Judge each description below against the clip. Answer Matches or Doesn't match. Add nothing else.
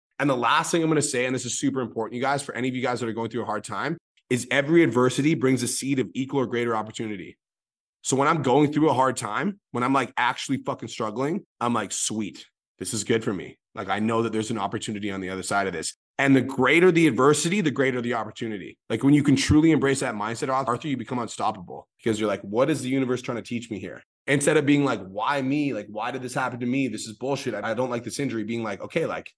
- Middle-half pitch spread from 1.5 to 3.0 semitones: Doesn't match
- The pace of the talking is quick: Matches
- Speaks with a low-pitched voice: Matches